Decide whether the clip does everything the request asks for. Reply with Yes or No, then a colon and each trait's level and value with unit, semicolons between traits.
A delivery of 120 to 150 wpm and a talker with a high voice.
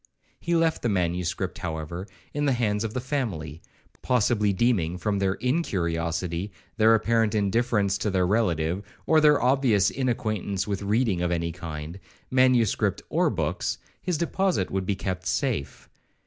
No: average, 145 wpm; low, 105 Hz